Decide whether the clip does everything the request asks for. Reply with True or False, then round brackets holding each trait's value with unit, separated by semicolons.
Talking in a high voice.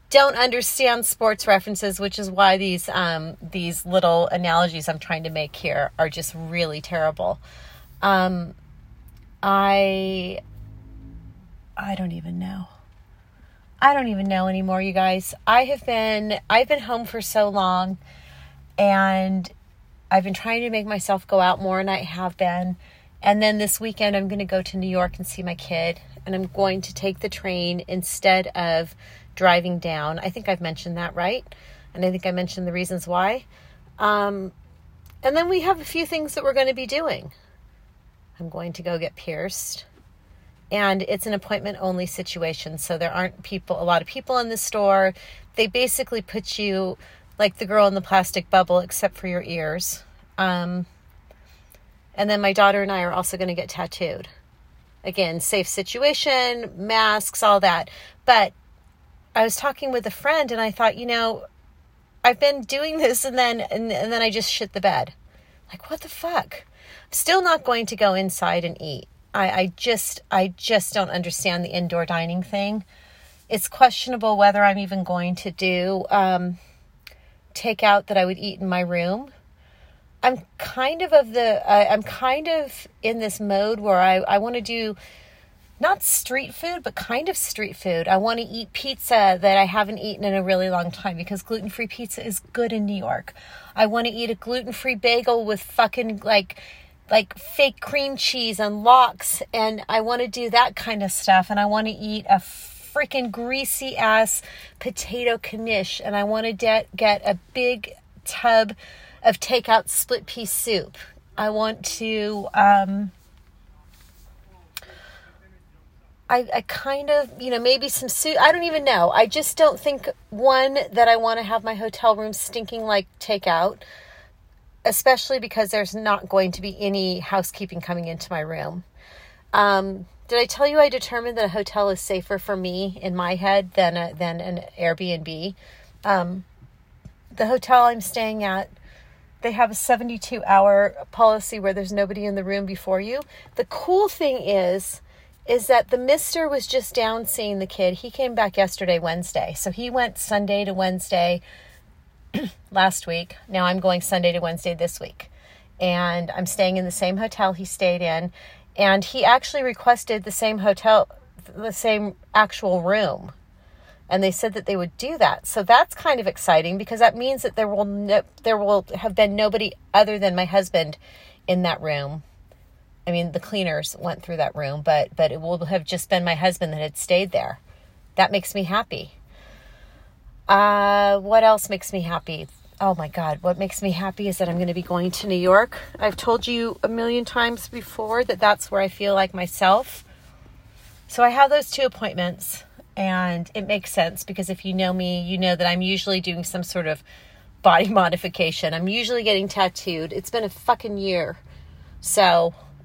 True (195 Hz)